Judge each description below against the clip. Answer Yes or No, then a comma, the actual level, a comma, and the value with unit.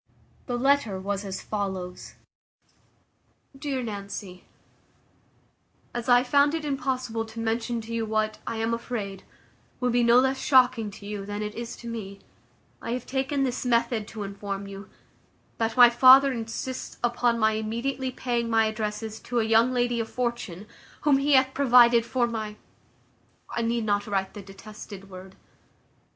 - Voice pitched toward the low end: No, high, 230 Hz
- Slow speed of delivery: No, average, 160 wpm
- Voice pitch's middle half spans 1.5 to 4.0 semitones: Yes, average, 3.1 semitones